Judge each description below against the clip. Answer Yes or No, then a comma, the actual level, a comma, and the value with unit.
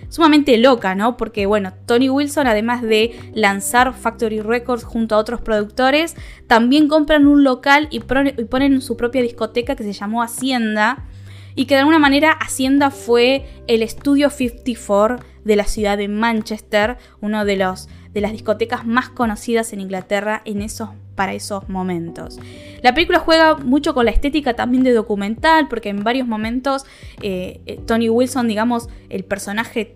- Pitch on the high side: Yes, high, 230 Hz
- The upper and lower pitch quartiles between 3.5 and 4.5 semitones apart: Yes, average, 3.9 semitones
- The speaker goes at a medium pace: Yes, average, 155 wpm